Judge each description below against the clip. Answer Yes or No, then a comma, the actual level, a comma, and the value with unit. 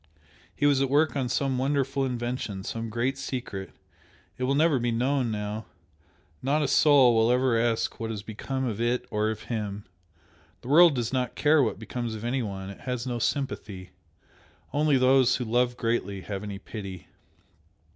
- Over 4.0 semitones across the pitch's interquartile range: No, average, 3.5 semitones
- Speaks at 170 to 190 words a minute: Yes, average, 175 wpm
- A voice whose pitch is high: No, low, 120 Hz